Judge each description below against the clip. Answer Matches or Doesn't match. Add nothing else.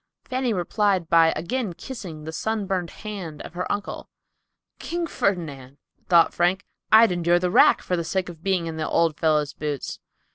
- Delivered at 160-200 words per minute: Matches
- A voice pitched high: Doesn't match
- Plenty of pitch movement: Doesn't match